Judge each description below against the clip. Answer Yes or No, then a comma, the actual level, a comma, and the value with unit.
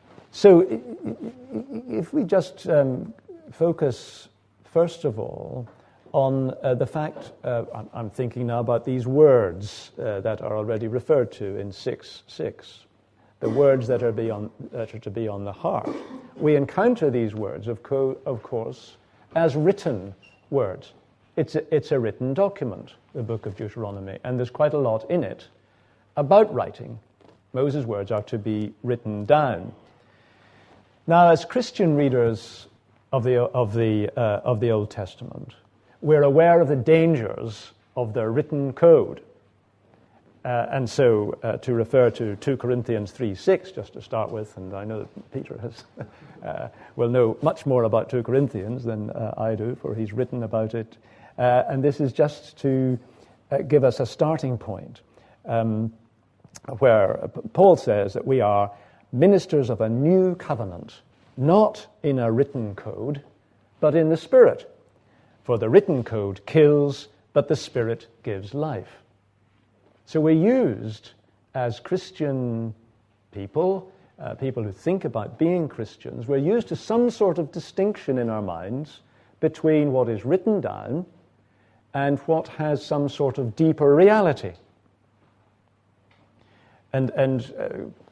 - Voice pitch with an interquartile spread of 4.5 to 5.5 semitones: Yes, average, 5.2 semitones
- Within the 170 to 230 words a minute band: No, average, 150 wpm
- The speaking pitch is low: Yes, low, 120 Hz